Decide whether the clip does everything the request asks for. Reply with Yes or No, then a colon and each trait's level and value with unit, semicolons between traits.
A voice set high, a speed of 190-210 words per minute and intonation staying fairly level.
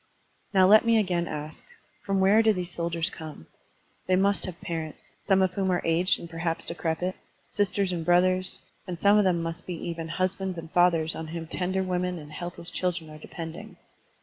No: medium, 175 Hz; average, 200 wpm; narrow, 2.2 semitones